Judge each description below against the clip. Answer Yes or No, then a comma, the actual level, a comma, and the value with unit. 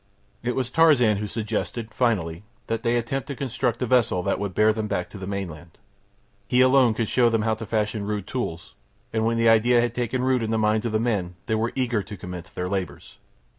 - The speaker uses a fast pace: Yes, fast, 225 wpm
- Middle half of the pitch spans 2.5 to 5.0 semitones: Yes, average, 3.0 semitones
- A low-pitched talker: Yes, low, 110 Hz